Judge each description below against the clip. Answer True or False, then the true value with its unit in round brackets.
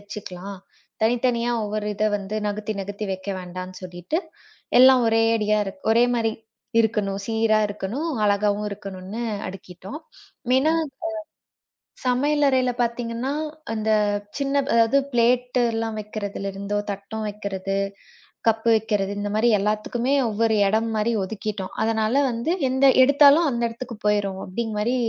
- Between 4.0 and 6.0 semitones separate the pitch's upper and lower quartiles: False (2.8 semitones)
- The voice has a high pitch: True (215 Hz)